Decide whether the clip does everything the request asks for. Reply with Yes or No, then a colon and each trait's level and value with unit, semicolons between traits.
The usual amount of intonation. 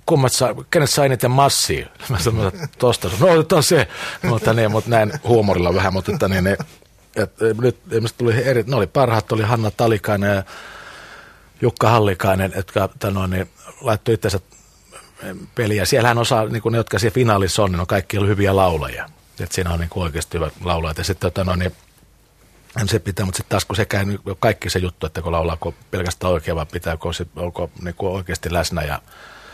Yes: average, 3.9 semitones